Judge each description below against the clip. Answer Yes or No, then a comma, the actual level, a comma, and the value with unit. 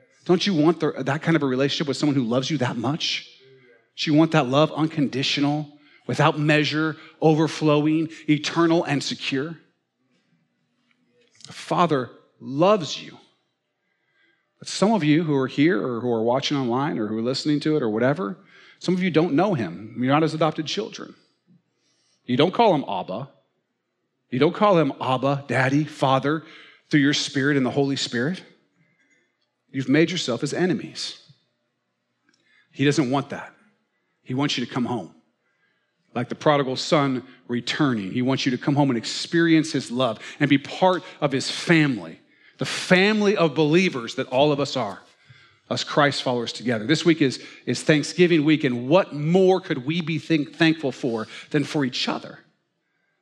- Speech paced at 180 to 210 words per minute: No, average, 170 wpm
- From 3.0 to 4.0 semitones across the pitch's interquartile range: Yes, average, 3.3 semitones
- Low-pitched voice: No, medium, 145 Hz